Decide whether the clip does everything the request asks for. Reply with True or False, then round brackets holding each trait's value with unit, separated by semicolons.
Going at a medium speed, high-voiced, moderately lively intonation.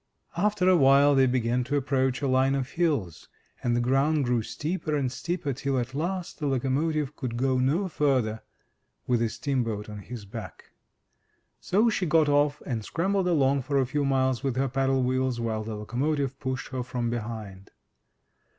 False (175 wpm; 135 Hz; 3.2 semitones)